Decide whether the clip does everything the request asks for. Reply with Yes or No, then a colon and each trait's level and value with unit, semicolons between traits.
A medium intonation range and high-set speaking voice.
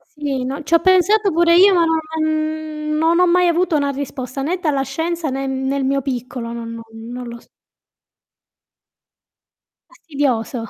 Yes: average, 4.4 semitones; very high, 290 Hz